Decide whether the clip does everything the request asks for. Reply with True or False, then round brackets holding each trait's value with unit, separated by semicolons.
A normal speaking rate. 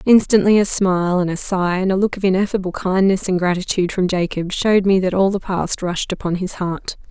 False (220 wpm)